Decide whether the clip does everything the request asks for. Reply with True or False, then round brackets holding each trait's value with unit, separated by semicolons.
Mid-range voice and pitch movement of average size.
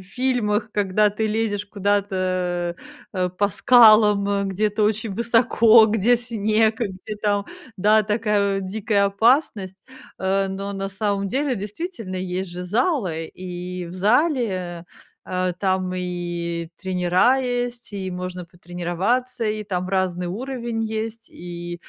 False (200 Hz; 3.4 semitones)